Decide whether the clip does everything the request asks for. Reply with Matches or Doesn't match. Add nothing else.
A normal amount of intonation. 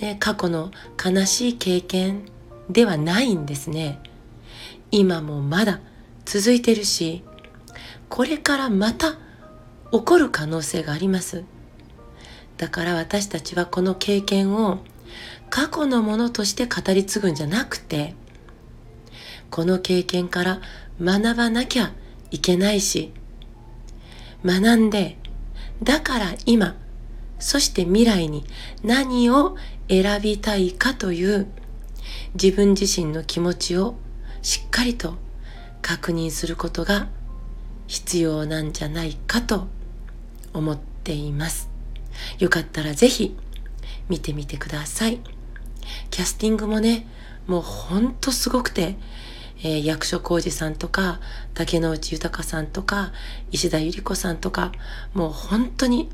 Matches